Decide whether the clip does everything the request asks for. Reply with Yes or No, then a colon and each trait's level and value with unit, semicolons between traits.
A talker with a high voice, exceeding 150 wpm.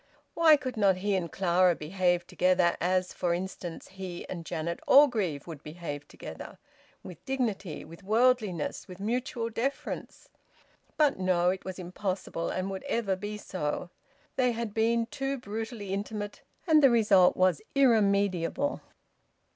No: high, 195 Hz; average, 140 wpm